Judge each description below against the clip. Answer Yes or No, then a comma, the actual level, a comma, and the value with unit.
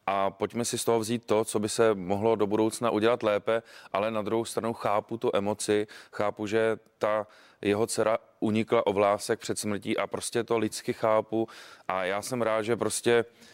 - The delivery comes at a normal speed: No, fast, 190 wpm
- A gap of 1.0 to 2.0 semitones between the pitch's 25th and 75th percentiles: Yes, narrow, 1.6 semitones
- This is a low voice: Yes, low, 110 Hz